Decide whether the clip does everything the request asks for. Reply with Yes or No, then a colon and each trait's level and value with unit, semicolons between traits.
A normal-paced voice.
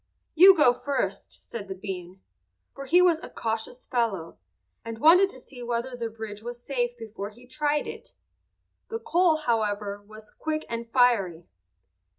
Yes: average, 160 wpm